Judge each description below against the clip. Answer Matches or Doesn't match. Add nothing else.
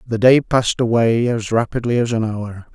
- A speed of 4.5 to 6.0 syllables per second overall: Matches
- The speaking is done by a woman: Doesn't match